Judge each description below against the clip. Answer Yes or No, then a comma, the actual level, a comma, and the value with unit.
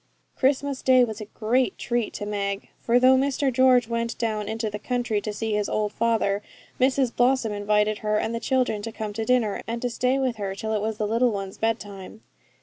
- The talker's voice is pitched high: Yes, high, 225 Hz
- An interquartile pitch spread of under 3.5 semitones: Yes, average, 3.1 semitones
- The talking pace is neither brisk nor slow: No, fast, 215 wpm